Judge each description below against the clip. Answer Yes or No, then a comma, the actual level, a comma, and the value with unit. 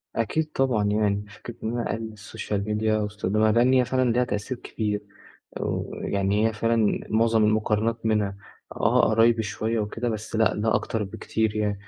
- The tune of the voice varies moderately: No, narrow, 1.6 semitones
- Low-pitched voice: Yes, low, 110 Hz